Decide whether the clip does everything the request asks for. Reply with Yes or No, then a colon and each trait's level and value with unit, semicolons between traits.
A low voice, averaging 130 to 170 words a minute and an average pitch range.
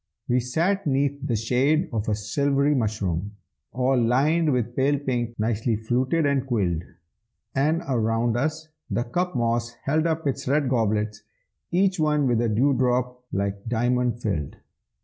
Yes: low, 125 Hz; average, 150 wpm; average, 4.0 semitones